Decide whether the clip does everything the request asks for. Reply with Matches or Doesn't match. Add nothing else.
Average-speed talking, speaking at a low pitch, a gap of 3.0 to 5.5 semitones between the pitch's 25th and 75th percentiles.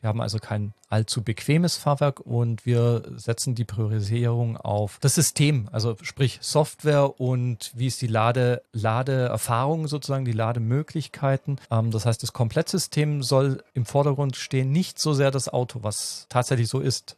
Matches